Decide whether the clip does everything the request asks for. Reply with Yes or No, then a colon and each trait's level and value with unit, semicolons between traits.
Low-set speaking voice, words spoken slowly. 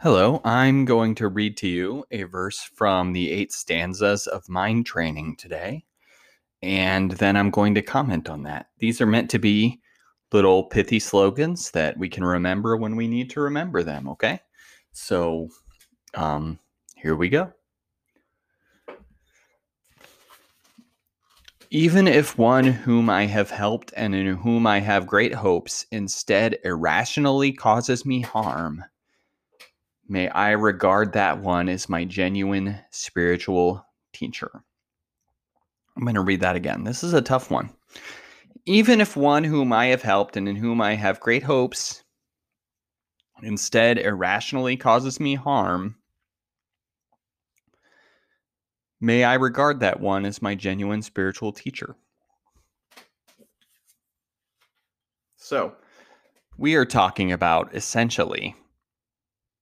Yes: low, 105 Hz; slow, 125 wpm